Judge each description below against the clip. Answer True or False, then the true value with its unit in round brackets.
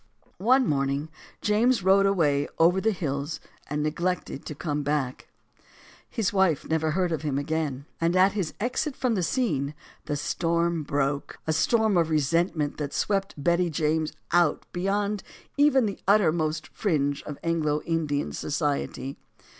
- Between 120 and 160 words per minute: True (145 wpm)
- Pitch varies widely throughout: False (4.6 semitones)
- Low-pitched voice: False (165 Hz)